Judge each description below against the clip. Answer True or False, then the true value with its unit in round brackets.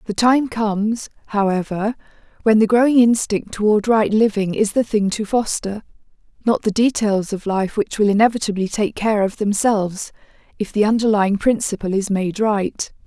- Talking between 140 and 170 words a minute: True (155 wpm)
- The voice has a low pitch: False (210 Hz)